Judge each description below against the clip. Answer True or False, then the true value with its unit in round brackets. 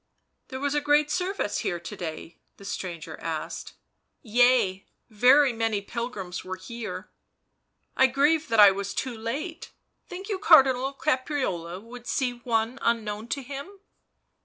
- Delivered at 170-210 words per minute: False (155 wpm)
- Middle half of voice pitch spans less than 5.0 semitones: False (5.4 semitones)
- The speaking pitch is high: True (240 Hz)